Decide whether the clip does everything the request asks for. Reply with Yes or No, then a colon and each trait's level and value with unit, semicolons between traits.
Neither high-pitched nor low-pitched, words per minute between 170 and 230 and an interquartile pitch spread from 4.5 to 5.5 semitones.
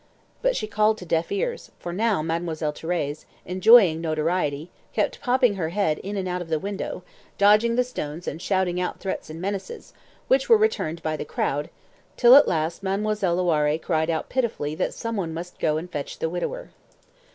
Yes: medium, 180 Hz; average, 185 wpm; average, 4.9 semitones